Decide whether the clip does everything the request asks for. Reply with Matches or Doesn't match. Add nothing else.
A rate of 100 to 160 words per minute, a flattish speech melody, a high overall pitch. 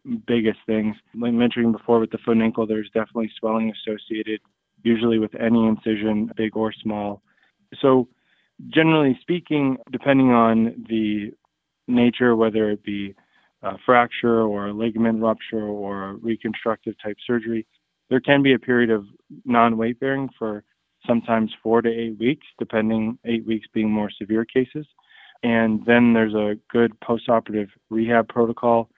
Doesn't match